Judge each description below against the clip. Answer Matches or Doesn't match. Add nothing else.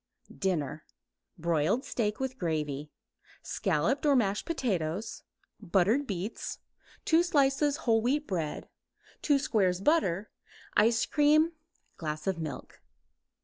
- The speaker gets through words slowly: Matches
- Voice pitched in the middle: Doesn't match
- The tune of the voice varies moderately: Doesn't match